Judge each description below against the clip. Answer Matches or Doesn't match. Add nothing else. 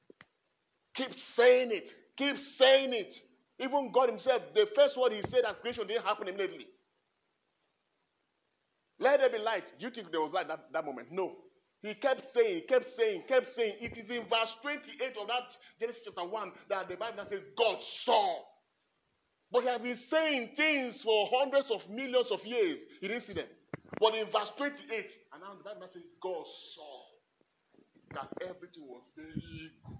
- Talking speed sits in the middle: Matches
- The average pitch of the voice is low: Doesn't match